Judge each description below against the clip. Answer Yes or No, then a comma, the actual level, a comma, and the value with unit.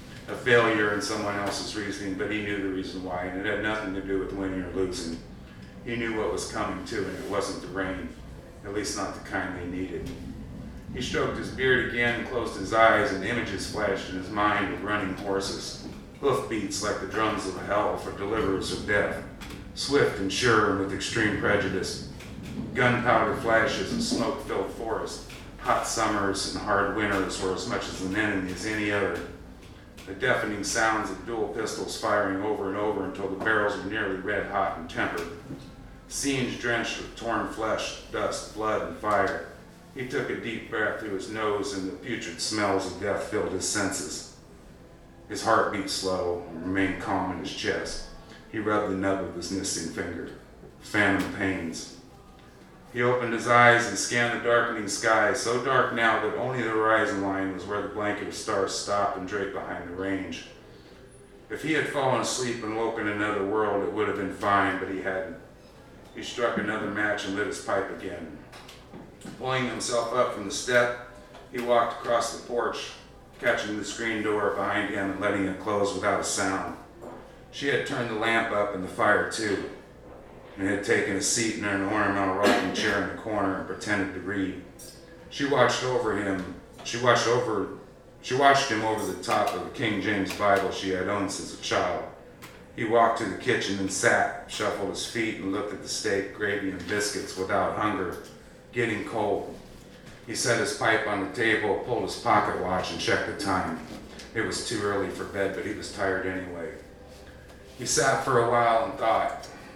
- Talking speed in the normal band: Yes, average, 190 wpm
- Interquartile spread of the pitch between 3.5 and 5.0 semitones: No, average, 2.9 semitones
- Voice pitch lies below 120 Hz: Yes, low, 100 Hz